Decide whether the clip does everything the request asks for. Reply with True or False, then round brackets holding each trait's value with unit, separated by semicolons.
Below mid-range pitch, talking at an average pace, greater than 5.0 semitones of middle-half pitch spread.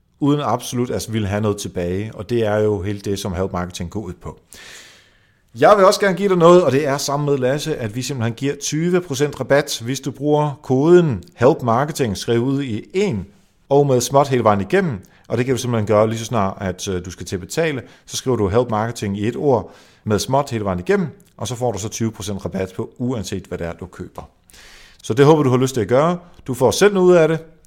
False (120 Hz; 240 wpm; 5.6 semitones)